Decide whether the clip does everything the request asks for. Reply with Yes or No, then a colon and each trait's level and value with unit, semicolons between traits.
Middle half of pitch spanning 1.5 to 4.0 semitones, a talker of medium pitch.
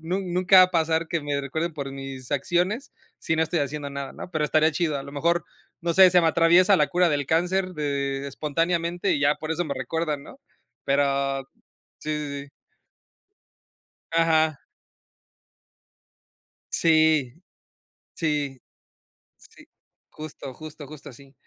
Yes: average, 3.2 semitones; medium, 155 Hz